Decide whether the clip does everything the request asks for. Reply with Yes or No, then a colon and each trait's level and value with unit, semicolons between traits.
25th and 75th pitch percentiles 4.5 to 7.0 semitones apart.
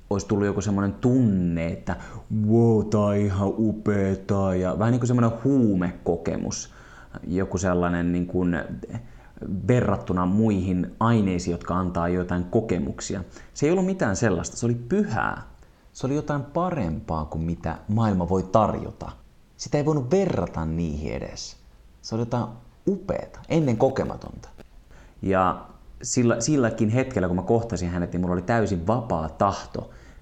Yes: average, 4.8 semitones